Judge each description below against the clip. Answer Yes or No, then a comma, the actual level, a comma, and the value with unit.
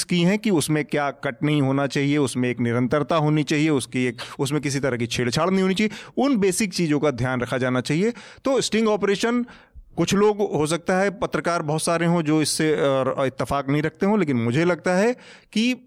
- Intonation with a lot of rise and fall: Yes, wide, 5.7 semitones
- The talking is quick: Yes, fast, 210 wpm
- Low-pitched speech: No, medium, 155 Hz